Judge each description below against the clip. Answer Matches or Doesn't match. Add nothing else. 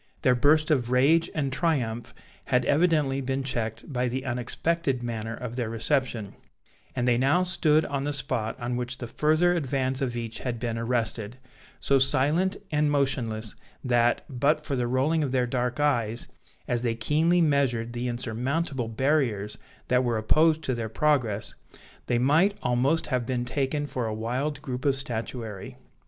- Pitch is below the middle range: Matches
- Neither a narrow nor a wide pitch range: Matches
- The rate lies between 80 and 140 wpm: Doesn't match